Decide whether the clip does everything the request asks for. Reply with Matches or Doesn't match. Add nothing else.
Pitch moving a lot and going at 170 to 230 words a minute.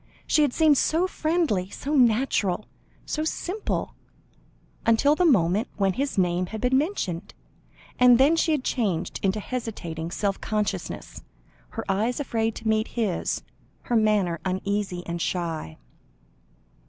Doesn't match